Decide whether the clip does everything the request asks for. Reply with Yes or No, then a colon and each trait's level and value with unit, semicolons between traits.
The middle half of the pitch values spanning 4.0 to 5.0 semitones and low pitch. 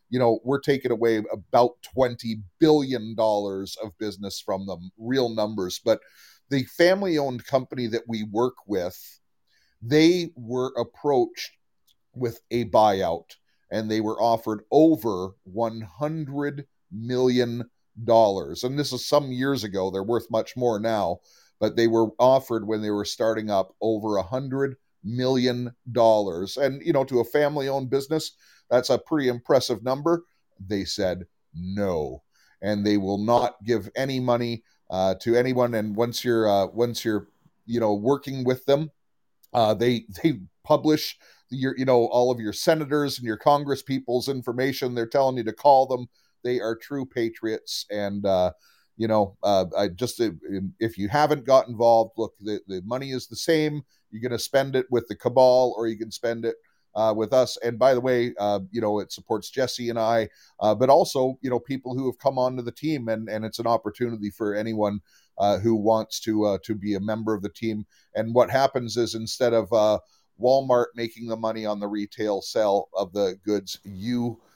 No: average, 3.3 semitones; low, 115 Hz